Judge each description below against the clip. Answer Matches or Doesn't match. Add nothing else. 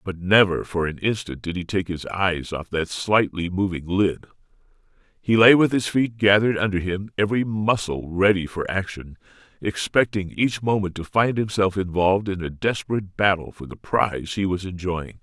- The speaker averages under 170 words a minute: Doesn't match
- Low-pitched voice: Matches